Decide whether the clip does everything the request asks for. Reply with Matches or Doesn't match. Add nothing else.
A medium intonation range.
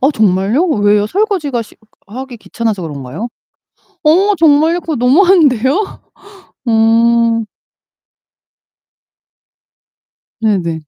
Doesn't match